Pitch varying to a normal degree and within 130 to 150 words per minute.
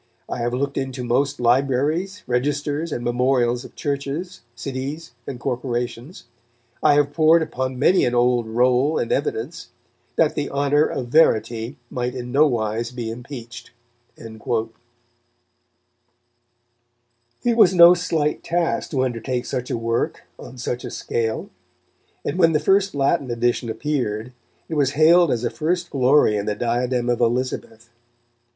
Yes: average, 3.7 semitones; average, 145 wpm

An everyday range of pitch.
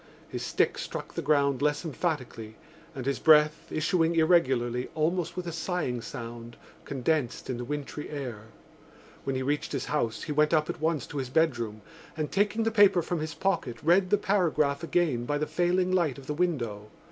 Yes: average, 4.9 semitones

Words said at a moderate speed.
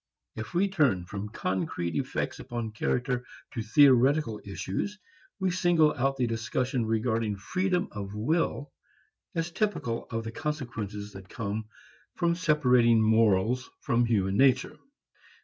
No: slow, 130 wpm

